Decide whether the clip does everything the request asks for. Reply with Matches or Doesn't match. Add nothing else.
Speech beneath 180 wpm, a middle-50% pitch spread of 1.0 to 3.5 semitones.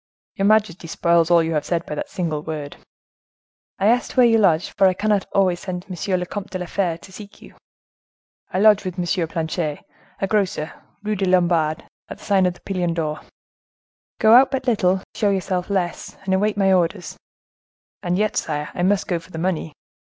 Doesn't match